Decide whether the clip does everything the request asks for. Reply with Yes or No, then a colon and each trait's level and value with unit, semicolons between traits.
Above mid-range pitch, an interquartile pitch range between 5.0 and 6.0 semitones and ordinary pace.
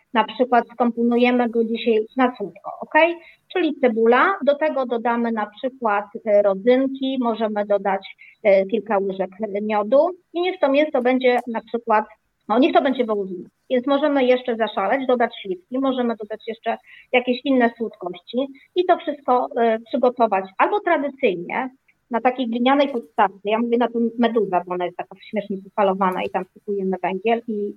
No: high, 235 Hz; average, 3.7 semitones; average, 150 wpm